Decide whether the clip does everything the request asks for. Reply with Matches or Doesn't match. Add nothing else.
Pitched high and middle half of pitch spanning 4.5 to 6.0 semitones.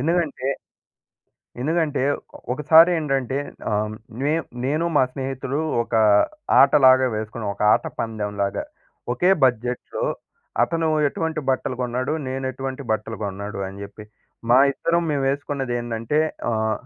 Doesn't match